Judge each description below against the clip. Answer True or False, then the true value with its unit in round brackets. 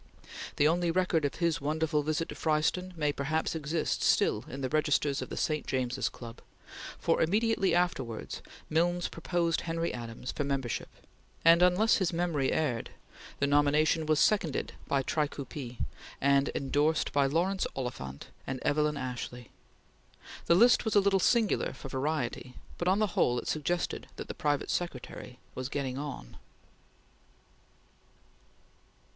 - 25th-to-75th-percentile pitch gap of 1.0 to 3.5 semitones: False (4.0 semitones)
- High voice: False (150 Hz)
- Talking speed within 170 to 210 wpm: False (145 wpm)